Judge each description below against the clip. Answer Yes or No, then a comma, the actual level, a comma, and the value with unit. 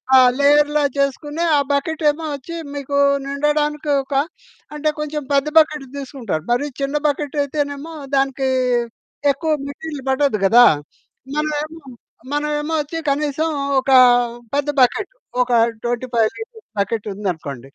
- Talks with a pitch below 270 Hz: No, very high, 285 Hz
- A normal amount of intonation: No, narrow, 2.1 semitones